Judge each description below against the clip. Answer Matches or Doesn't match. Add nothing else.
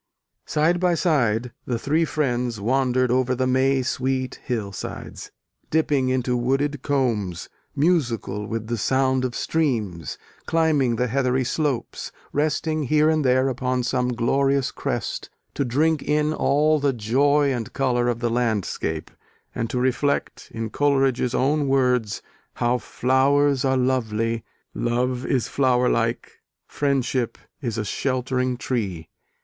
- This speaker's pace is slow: Matches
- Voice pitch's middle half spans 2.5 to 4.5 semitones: Matches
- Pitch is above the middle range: Doesn't match